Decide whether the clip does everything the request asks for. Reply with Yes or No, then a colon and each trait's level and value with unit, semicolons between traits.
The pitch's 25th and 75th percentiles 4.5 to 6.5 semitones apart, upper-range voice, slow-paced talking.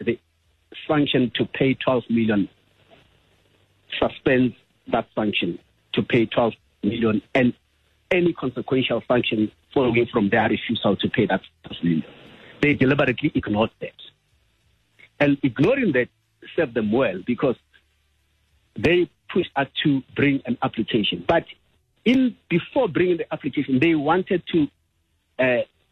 No: average, 5.0 semitones; low, 120 Hz; slow, 125 wpm